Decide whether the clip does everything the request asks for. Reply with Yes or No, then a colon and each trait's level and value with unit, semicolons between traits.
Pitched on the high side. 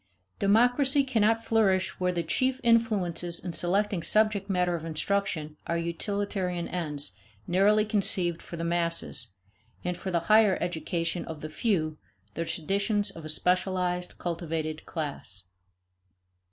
No: medium, 180 Hz